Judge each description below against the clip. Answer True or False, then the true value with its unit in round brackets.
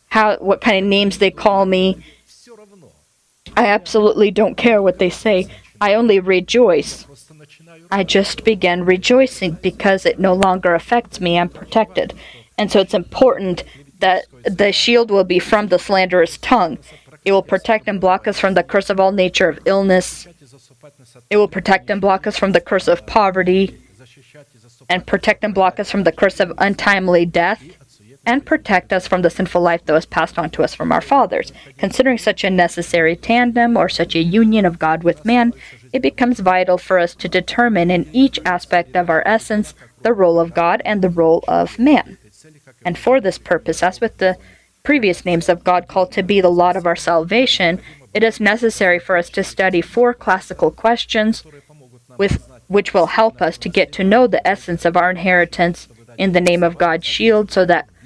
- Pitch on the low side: False (185 Hz)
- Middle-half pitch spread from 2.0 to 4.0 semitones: True (3.4 semitones)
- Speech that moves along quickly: False (185 wpm)